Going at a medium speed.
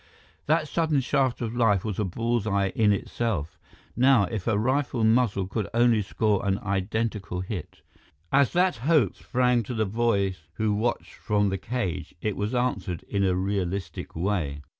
Yes: average, 165 wpm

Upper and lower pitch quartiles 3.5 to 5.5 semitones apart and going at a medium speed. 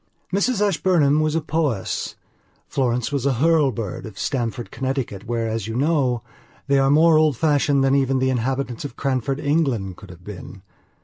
Yes: average, 4.2 semitones; average, 170 wpm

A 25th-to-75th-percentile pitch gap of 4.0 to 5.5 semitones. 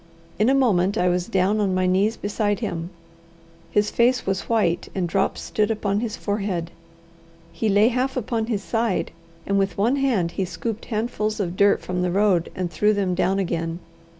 No: average, 3.2 semitones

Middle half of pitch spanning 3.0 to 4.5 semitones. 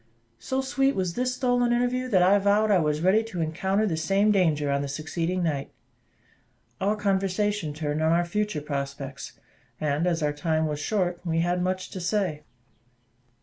No: average, 4.9 semitones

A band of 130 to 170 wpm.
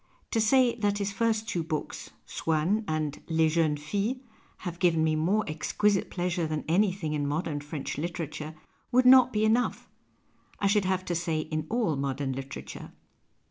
No: average, 180 wpm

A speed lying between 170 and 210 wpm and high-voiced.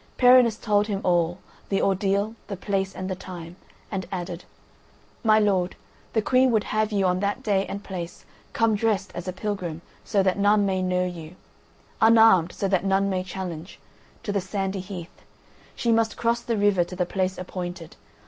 Yes: average, 175 wpm; high, 195 Hz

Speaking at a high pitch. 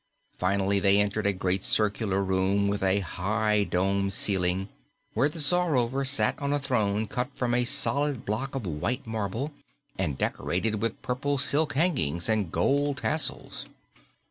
No: low, 105 Hz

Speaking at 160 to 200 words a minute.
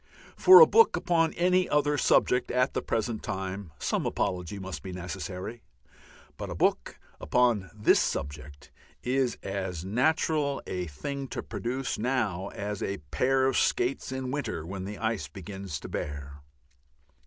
No: average, 150 wpm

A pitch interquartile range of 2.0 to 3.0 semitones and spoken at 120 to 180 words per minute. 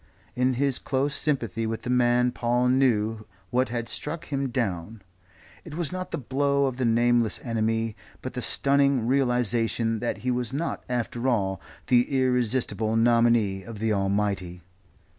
Yes: narrow, 2.6 semitones; average, 155 wpm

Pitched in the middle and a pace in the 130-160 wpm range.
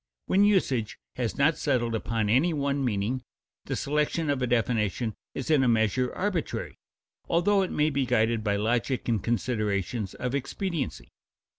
No: low, 125 Hz; average, 155 wpm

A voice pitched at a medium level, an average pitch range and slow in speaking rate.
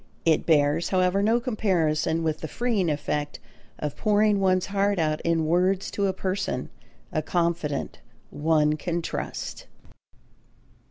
Yes: medium, 170 Hz; average, 4.1 semitones; slow, 130 wpm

